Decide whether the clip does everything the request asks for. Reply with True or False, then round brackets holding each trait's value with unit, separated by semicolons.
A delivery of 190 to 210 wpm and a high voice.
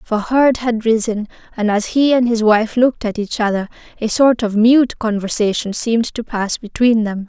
True (200 wpm; 225 Hz)